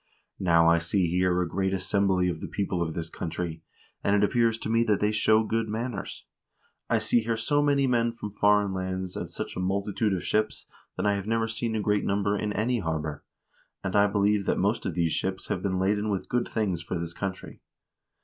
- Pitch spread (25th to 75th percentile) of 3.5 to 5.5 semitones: No, average, 3.0 semitones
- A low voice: Yes, low, 100 Hz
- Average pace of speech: No, fast, 215 wpm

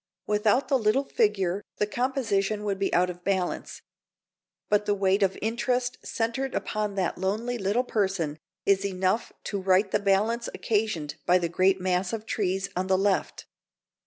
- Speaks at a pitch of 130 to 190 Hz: No, high, 200 Hz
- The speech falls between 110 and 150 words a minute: No, average, 160 wpm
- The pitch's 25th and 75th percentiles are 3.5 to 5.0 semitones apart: No, average, 2.8 semitones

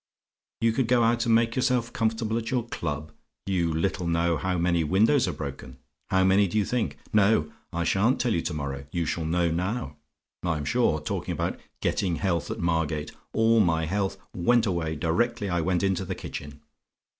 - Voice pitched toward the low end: Yes, very low, 90 Hz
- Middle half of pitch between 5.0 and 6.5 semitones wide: Yes, wide, 5.5 semitones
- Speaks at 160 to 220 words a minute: Yes, average, 190 wpm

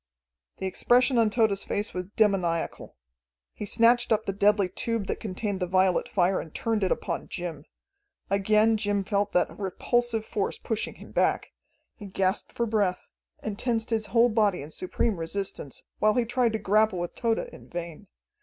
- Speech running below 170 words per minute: No, average, 175 wpm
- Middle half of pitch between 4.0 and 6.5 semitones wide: No, average, 3.1 semitones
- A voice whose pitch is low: No, high, 205 Hz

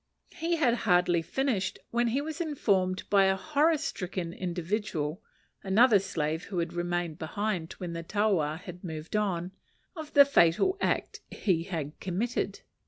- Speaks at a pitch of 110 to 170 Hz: No, high, 190 Hz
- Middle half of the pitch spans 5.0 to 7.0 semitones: Yes, wide, 5.6 semitones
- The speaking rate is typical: Yes, average, 150 wpm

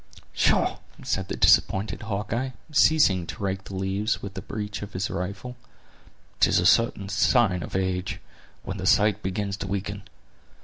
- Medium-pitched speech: No, low, 100 Hz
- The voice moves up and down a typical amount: No, narrow, 1.8 semitones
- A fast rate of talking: No, average, 160 wpm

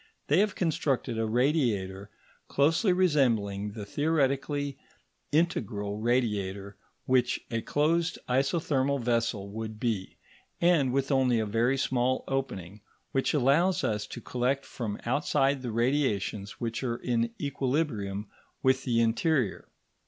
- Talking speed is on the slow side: Yes, slow, 125 wpm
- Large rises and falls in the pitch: No, average, 4.4 semitones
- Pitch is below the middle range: Yes, low, 125 Hz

